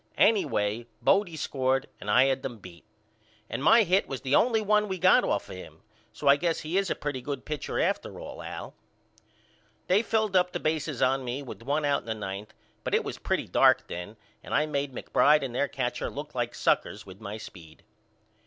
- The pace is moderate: No, fast, 210 wpm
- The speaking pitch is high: No, medium, 140 Hz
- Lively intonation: Yes, wide, 6.0 semitones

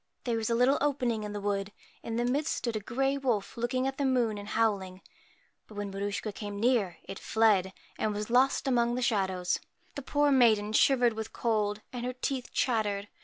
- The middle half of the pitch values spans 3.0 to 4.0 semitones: Yes, average, 3.5 semitones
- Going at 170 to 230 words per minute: Yes, fast, 205 wpm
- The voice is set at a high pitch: Yes, high, 225 Hz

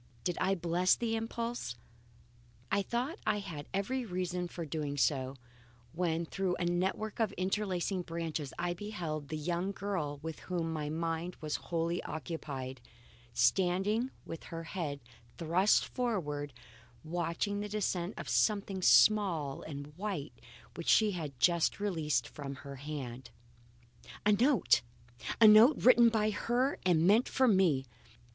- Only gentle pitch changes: No, average, 5.0 semitones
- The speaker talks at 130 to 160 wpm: Yes, average, 140 wpm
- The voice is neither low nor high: Yes, medium, 175 Hz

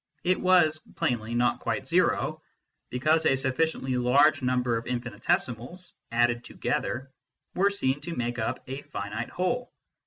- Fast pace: No, slow, 135 wpm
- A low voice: Yes, low, 130 Hz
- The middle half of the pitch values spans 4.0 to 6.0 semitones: Yes, average, 5.1 semitones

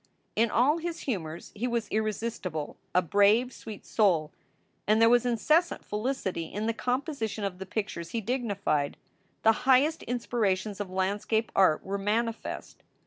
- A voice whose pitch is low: No, high, 215 Hz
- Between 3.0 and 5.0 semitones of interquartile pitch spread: Yes, average, 3.9 semitones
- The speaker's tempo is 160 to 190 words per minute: No, average, 145 wpm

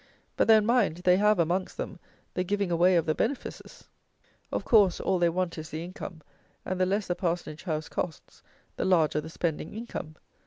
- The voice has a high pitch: No, medium, 180 Hz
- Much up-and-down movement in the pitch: No, average, 3.1 semitones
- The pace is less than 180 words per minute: No, average, 190 wpm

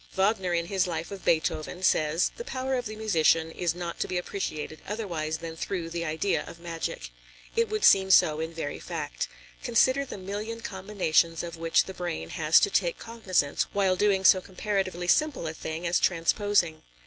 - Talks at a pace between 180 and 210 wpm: Yes, average, 185 wpm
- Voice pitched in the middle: Yes, medium, 180 Hz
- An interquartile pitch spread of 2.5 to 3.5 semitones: No, average, 3.9 semitones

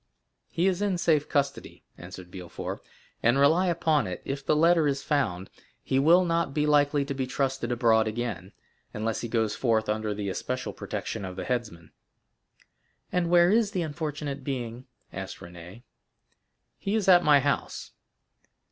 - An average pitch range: No, wide, 6.5 semitones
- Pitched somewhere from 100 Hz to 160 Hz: Yes, low, 135 Hz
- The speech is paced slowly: No, average, 160 wpm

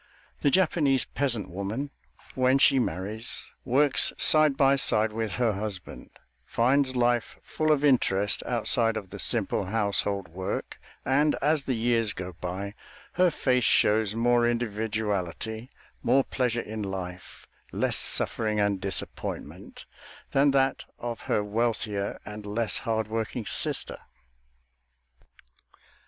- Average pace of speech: No, slow, 125 wpm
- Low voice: Yes, low, 115 Hz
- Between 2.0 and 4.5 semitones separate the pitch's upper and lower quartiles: Yes, average, 4.2 semitones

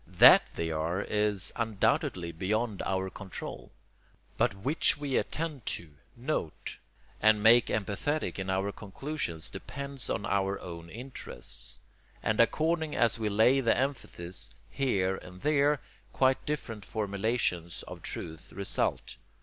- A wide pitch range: Yes, wide, 5.9 semitones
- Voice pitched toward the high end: No, low, 105 Hz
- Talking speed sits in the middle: No, slow, 125 wpm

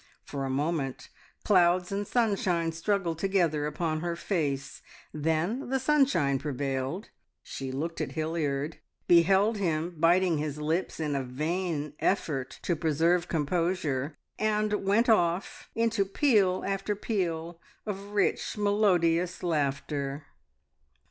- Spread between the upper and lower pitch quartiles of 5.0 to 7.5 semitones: No, average, 4.6 semitones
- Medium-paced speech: No, slow, 120 wpm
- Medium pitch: Yes, medium, 170 Hz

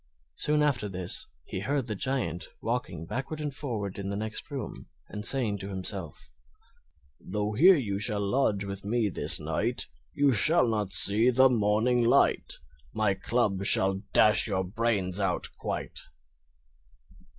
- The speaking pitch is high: No, low, 105 Hz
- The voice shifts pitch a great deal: No, average, 4.1 semitones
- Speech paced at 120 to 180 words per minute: Yes, average, 150 wpm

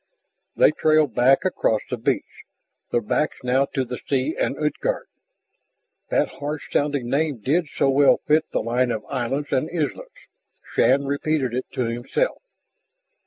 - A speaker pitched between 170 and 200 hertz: No, medium, 140 Hz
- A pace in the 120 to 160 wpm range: Yes, average, 150 wpm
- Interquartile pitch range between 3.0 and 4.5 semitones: Yes, average, 3.3 semitones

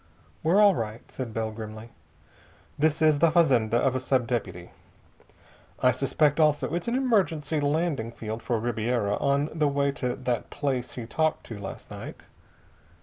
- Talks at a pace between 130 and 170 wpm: Yes, average, 160 wpm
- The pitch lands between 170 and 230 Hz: No, low, 135 Hz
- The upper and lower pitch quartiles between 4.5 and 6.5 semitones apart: Yes, average, 5.2 semitones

